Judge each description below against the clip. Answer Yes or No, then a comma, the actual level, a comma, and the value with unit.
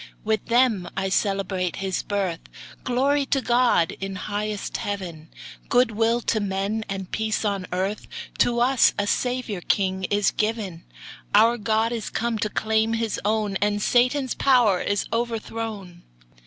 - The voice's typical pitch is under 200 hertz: No, high, 215 Hz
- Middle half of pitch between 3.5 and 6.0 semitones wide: No, average, 3.1 semitones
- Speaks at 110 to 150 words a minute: Yes, average, 145 wpm